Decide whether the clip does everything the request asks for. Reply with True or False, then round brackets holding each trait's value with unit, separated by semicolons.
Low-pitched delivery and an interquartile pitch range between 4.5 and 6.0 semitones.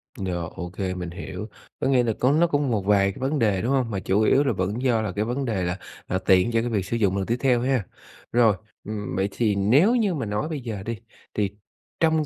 True (110 Hz; 4.9 semitones)